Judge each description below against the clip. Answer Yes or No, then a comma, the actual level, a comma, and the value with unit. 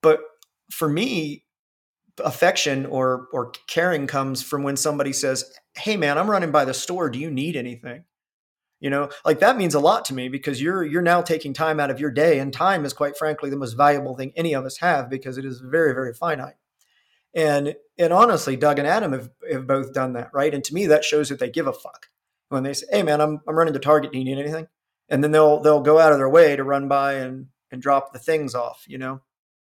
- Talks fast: Yes, fast, 235 wpm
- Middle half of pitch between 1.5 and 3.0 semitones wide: Yes, narrow, 2.6 semitones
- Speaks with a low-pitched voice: No, medium, 145 Hz